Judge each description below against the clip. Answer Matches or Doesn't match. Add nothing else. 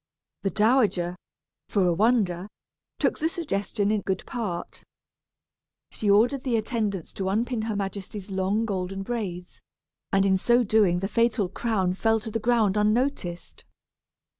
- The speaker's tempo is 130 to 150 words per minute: Matches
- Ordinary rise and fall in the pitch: Matches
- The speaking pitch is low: Doesn't match